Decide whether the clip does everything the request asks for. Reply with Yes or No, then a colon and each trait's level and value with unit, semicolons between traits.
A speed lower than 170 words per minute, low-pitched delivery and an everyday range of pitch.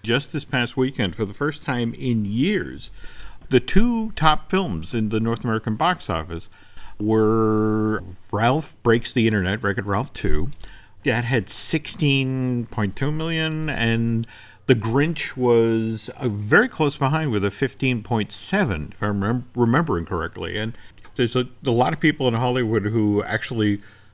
Yes: average, 145 wpm; low, 115 Hz; average, 4.1 semitones